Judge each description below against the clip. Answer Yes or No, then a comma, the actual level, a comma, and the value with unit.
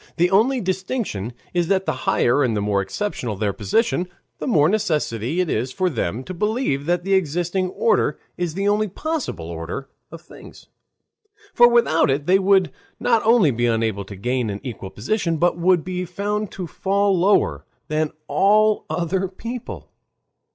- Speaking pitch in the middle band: Yes, medium, 175 Hz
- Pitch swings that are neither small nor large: No, wide, 7.7 semitones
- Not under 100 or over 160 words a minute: No, average, 170 wpm